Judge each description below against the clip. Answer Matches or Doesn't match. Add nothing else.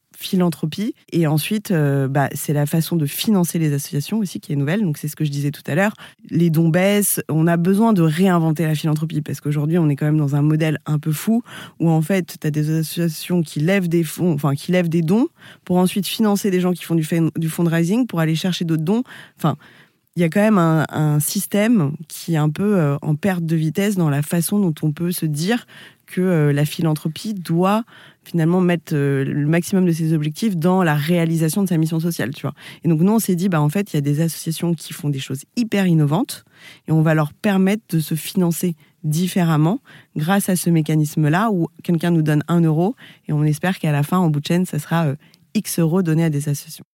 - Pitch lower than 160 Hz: Doesn't match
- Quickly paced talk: Matches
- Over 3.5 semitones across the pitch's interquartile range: Doesn't match